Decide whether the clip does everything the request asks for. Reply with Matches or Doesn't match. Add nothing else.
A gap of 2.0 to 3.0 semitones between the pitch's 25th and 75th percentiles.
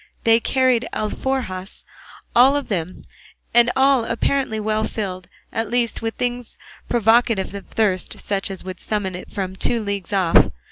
Doesn't match